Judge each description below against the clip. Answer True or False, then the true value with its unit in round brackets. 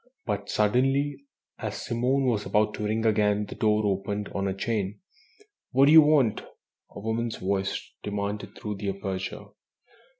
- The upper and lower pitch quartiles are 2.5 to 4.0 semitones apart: True (3.0 semitones)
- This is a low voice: True (105 Hz)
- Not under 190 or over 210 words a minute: False (155 wpm)